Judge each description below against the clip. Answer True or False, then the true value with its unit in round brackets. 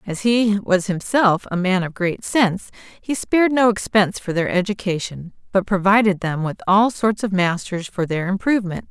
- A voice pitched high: True (195 Hz)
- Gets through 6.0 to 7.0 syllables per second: False (4.9 syllables/s)